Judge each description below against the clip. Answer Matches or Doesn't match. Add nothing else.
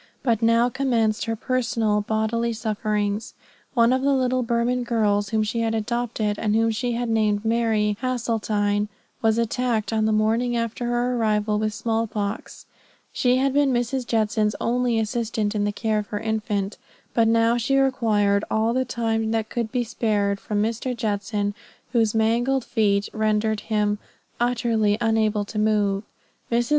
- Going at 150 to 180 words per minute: Matches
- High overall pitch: Matches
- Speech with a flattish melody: Matches